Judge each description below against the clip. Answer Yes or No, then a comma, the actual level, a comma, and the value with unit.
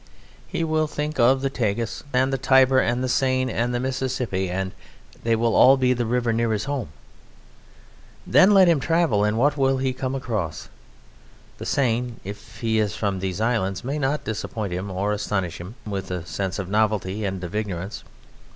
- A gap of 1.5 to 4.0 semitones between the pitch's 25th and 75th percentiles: No, average, 4.8 semitones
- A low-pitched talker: Yes, low, 115 Hz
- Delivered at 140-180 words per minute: No, average, 190 wpm